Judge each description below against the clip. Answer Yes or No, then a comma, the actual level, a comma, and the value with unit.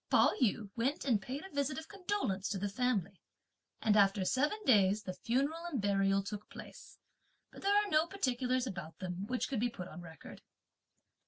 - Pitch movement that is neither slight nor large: No, wide, 6.3 semitones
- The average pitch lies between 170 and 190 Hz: No, high, 230 Hz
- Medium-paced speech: Yes, average, 185 wpm